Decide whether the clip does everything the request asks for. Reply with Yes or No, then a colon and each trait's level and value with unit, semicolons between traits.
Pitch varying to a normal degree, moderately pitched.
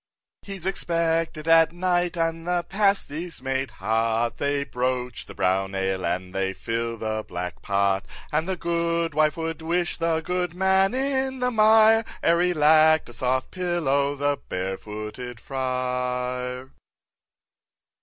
No: wide, 6.1 semitones; medium, 150 Hz